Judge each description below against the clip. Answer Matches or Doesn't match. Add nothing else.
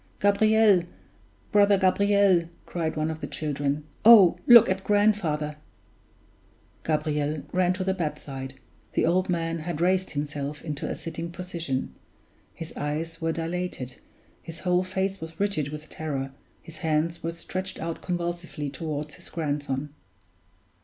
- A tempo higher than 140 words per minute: Doesn't match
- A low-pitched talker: Doesn't match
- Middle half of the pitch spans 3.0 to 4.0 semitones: Matches